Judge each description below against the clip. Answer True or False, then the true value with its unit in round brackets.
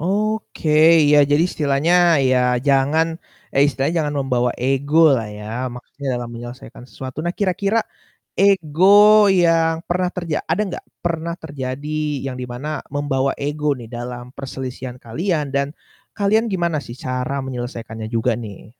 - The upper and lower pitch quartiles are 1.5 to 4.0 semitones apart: False (4.7 semitones)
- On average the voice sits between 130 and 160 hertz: True (140 Hz)